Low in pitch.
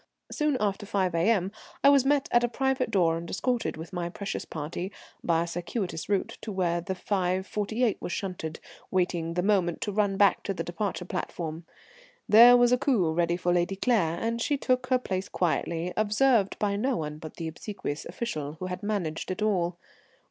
No: high, 190 Hz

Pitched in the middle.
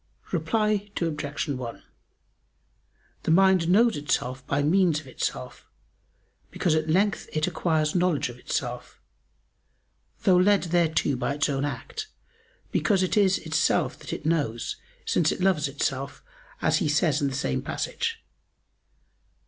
Yes: medium, 160 Hz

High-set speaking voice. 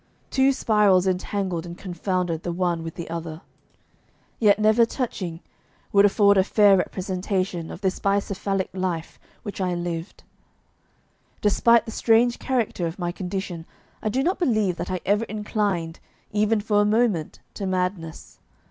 Yes: high, 195 Hz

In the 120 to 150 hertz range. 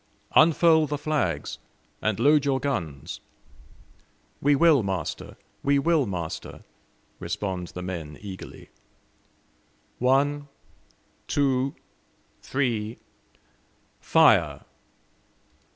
Yes: low, 135 Hz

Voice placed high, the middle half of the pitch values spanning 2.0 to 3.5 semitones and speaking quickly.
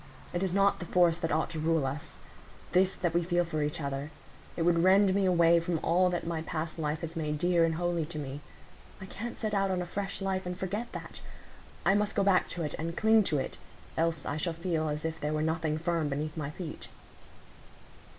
No: medium, 170 Hz; average, 2.8 semitones; fast, 225 wpm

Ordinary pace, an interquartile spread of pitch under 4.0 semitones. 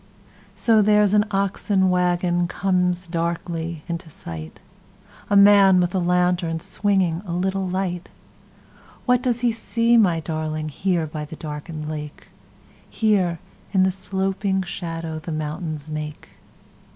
No: slow, 105 wpm; average, 3.1 semitones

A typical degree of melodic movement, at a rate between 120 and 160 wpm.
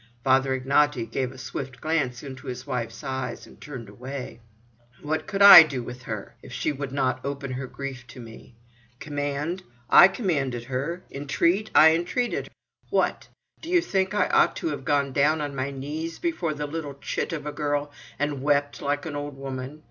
No: average, 3.0 semitones; average, 185 wpm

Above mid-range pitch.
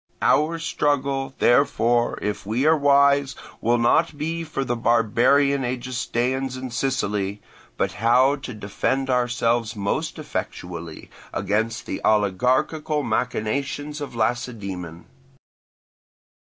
No: low, 125 Hz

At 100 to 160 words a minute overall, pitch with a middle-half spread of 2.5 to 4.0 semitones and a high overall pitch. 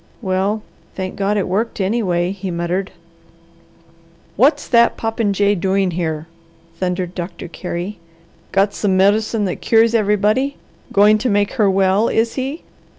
Yes: slow, 135 wpm; average, 2.8 semitones; high, 200 Hz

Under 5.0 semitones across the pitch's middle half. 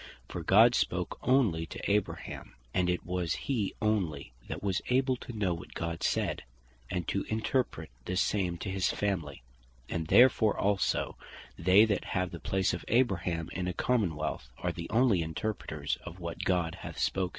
Yes: average, 4.1 semitones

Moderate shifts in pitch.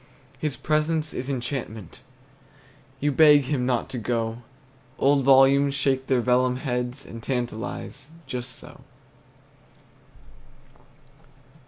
No: narrow, 2.3 semitones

